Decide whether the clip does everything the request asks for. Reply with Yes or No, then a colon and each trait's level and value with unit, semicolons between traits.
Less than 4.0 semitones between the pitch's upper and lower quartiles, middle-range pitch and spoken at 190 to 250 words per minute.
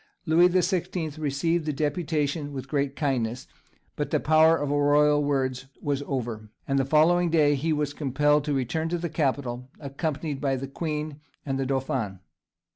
No: average, 2.7 semitones; medium, 145 Hz; average, 170 wpm